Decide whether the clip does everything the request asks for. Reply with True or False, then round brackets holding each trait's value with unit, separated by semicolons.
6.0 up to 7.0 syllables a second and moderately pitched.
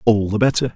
False (6.4 syllables/s; 115 Hz)